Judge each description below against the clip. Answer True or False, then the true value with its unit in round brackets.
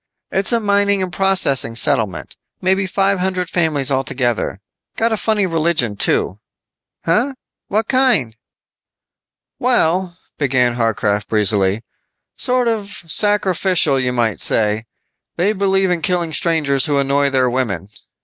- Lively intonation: True (7.6 semitones)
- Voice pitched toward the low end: False (165 Hz)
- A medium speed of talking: False (125 wpm)